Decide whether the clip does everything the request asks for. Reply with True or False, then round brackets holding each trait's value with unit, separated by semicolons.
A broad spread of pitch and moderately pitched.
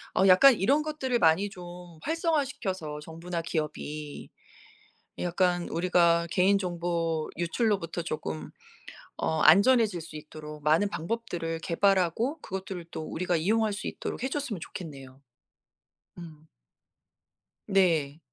False (4.0 semitones; 175 Hz)